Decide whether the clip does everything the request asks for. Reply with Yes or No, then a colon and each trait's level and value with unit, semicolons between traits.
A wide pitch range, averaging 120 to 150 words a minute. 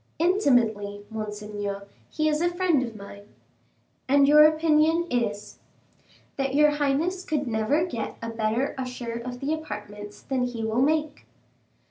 Yes: wide, 5.9 semitones; average, 140 wpm